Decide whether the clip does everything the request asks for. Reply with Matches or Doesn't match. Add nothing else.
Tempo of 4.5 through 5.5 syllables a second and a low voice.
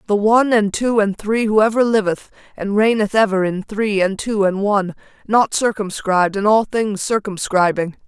Doesn't match